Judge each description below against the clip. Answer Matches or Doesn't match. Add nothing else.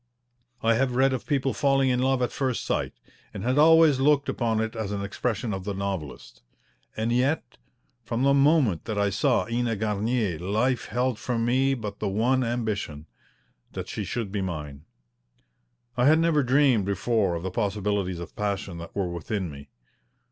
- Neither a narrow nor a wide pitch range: Matches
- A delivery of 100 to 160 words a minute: Doesn't match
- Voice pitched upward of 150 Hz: Doesn't match